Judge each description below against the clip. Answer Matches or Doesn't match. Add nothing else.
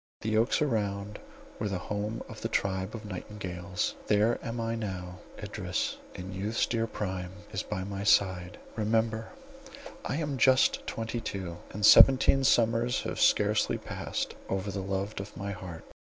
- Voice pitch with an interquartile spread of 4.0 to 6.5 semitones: Doesn't match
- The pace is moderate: Matches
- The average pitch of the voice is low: Matches